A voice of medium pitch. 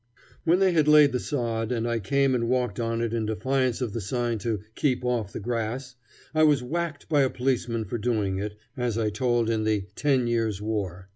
No: low, 120 Hz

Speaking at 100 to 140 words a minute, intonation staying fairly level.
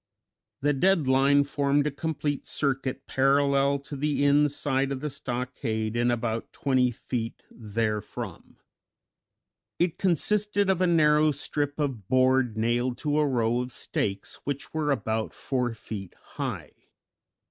No: slow, 135 wpm; average, 3.3 semitones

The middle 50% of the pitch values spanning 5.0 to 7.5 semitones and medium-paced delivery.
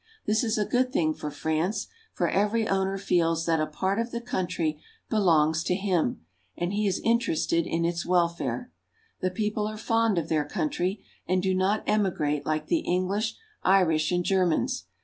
No: average, 4.3 semitones; average, 175 wpm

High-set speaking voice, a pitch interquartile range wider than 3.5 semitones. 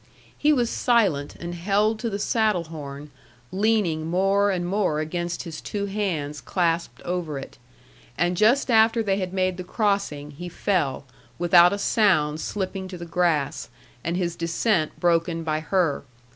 No: medium, 180 Hz; average, 3.9 semitones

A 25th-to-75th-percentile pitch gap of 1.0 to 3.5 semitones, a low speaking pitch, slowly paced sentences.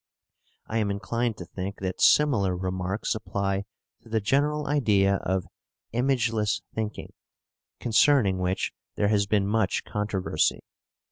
Yes: average, 2.9 semitones; low, 105 Hz; slow, 125 wpm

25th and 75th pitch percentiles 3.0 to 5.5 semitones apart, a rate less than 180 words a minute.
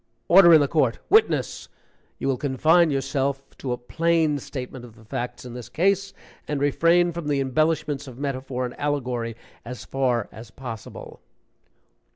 Yes: average, 4.0 semitones; average, 160 wpm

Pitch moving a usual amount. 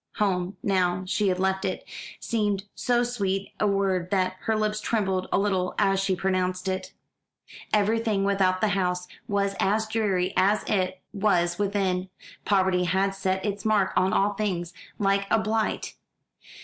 No: narrow, 2.0 semitones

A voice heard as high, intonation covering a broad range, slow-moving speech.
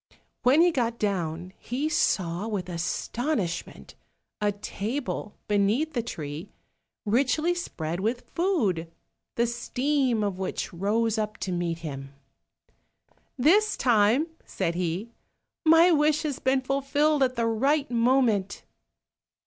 Yes: high, 230 Hz; wide, 6.7 semitones; slow, 120 wpm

